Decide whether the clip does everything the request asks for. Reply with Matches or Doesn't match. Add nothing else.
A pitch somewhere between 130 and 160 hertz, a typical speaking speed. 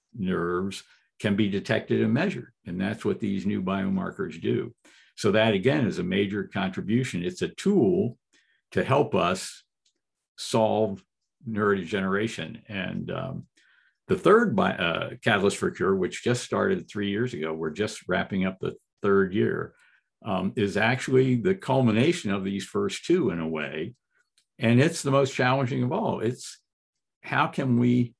Doesn't match